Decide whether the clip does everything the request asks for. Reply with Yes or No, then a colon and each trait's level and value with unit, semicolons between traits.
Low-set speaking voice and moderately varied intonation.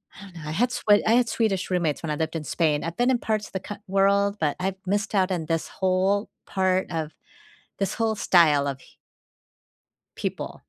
No: high, 190 Hz; average, 3.7 semitones